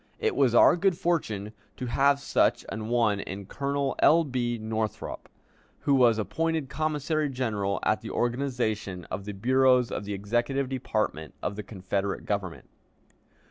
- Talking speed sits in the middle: Yes, average, 150 wpm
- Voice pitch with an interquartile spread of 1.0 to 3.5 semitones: No, average, 5.2 semitones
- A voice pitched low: Yes, low, 120 Hz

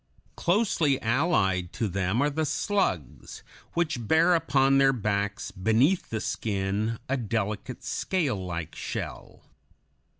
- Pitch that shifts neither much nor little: No, wide, 6.9 semitones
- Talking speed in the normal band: No, slow, 120 wpm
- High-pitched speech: No, low, 115 Hz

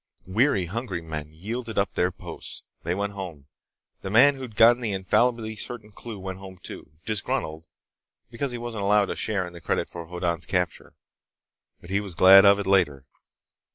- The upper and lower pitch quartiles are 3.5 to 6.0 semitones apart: Yes, average, 4.1 semitones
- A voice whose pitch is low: Yes, low, 100 Hz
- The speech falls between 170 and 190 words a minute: Yes, average, 180 wpm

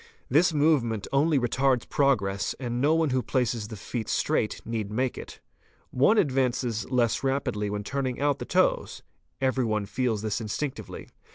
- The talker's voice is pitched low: Yes, low, 125 Hz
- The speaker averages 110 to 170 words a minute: Yes, average, 160 wpm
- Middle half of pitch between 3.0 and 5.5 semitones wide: Yes, average, 3.8 semitones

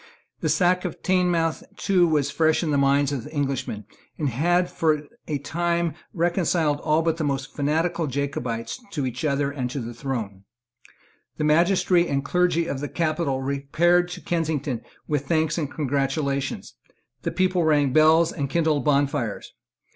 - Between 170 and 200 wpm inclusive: No, average, 155 wpm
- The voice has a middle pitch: Yes, medium, 150 Hz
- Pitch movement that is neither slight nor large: Yes, average, 3.4 semitones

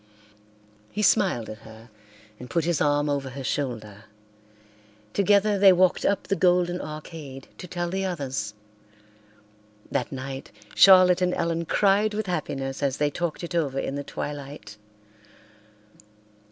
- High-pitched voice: No, medium, 155 Hz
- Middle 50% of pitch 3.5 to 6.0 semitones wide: Yes, average, 5.3 semitones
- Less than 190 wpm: Yes, average, 140 wpm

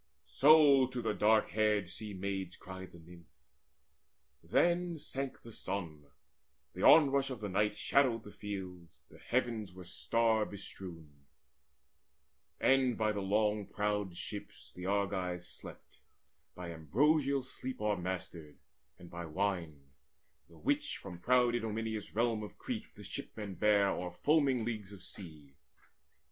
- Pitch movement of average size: Yes, average, 4.7 semitones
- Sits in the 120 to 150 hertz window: No, low, 105 Hz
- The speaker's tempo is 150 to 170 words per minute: No, slow, 135 wpm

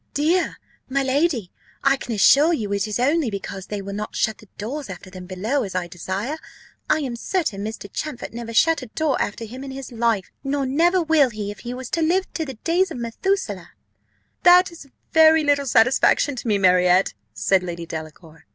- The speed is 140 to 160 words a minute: No, average, 195 wpm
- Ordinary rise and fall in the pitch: No, wide, 7.0 semitones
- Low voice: No, high, 240 Hz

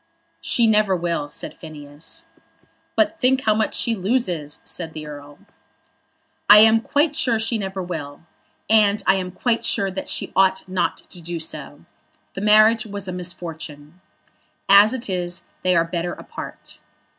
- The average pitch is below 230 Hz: Yes, high, 190 Hz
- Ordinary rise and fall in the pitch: Yes, average, 4.6 semitones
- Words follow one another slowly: No, average, 155 wpm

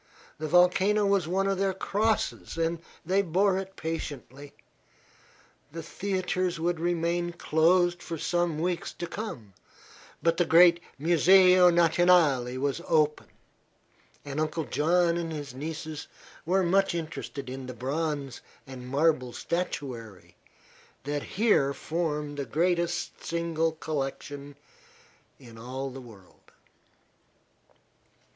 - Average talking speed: No, slow, 115 wpm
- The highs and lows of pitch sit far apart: No, average, 3.7 semitones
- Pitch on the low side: No, medium, 165 Hz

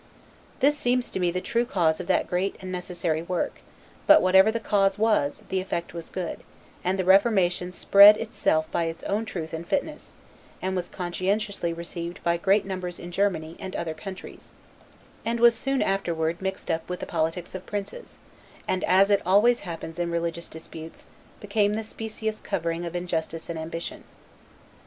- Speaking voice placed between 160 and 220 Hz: Yes, medium, 185 Hz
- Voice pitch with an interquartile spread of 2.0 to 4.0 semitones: Yes, average, 3.1 semitones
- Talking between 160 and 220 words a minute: Yes, average, 170 wpm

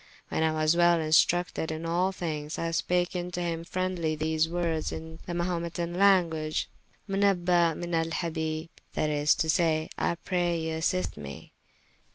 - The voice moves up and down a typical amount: No, narrow, 1.8 semitones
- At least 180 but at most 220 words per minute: No, average, 150 wpm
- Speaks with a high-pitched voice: No, medium, 165 Hz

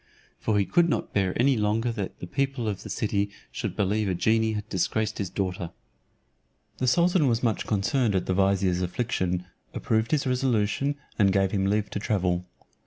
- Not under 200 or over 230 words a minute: No, average, 180 wpm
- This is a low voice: Yes, low, 105 Hz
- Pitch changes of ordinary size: Yes, average, 3.6 semitones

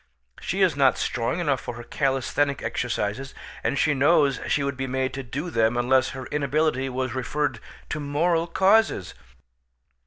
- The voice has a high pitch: No, low, 135 Hz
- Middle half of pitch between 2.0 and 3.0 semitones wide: Yes, average, 2.7 semitones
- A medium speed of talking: Yes, average, 160 wpm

